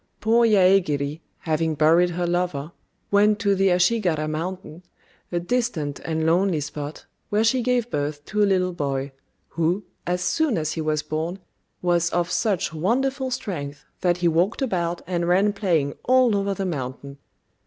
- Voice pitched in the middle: Yes, medium, 175 Hz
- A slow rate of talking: No, average, 160 wpm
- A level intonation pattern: No, average, 4.5 semitones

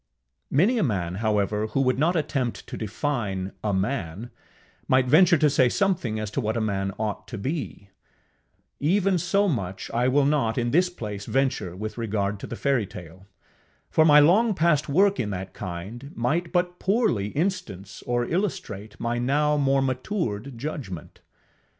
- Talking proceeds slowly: No, average, 160 wpm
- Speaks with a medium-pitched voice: No, low, 125 Hz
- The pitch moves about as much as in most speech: No, wide, 6.8 semitones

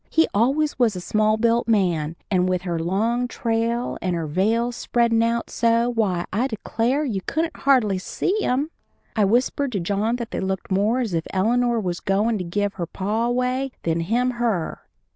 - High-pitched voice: Yes, high, 225 Hz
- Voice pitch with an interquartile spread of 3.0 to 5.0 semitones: Yes, average, 4.2 semitones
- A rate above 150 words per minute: Yes, average, 185 wpm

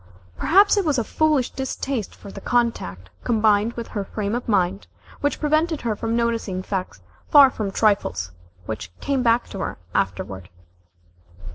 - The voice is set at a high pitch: Yes, high, 225 Hz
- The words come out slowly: No, average, 155 wpm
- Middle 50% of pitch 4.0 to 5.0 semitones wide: No, wide, 5.4 semitones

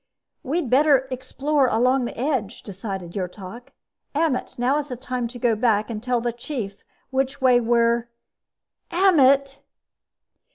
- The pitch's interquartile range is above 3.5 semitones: No, average, 2.8 semitones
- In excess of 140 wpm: No, slow, 135 wpm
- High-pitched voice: Yes, very high, 250 Hz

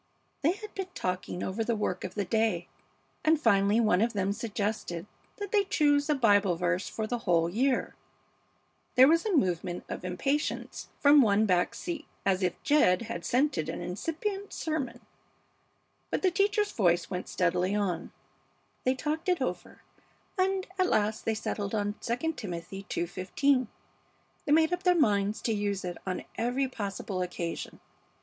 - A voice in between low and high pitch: No, high, 220 Hz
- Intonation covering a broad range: Yes, wide, 8.2 semitones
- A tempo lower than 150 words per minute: No, average, 165 wpm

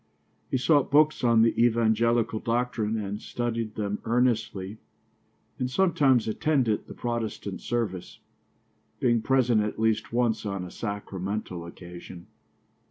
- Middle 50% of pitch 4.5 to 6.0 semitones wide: No, average, 2.7 semitones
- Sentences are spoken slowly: Yes, slow, 120 wpm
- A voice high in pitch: No, low, 115 Hz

